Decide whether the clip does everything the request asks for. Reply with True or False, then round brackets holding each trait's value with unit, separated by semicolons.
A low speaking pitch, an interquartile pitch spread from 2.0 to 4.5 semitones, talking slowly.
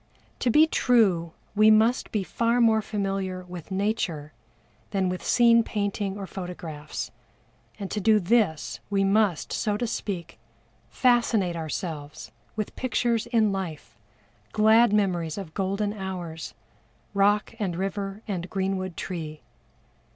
False (195 Hz; 3.3 semitones; 130 wpm)